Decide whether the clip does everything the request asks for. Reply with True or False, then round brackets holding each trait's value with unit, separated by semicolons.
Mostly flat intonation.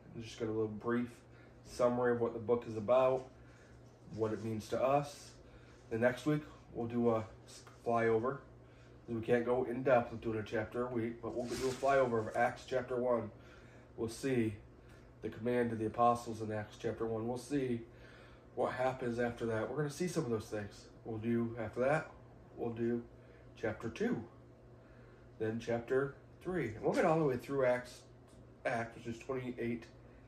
True (1.6 semitones)